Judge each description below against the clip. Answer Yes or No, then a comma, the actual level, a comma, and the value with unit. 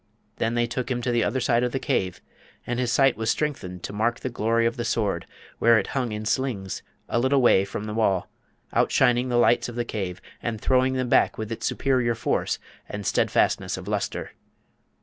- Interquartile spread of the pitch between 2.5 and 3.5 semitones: Yes, average, 2.8 semitones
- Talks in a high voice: No, low, 120 Hz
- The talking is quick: Yes, fast, 210 wpm